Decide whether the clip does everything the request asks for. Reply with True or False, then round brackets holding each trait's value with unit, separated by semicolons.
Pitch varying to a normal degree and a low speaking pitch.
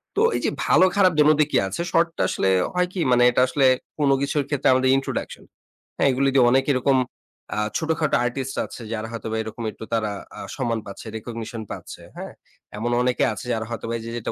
True (3.9 semitones; 125 Hz)